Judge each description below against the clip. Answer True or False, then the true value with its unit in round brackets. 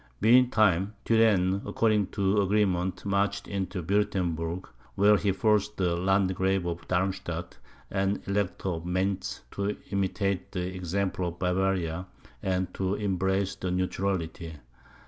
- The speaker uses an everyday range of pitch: False (1.8 semitones)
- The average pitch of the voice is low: True (95 Hz)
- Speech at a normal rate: False (125 wpm)